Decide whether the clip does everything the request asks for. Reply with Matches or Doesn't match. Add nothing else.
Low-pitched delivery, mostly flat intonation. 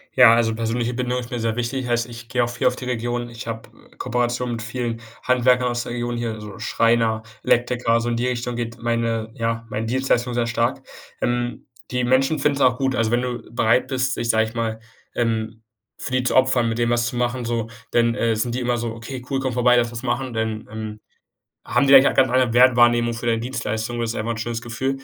Matches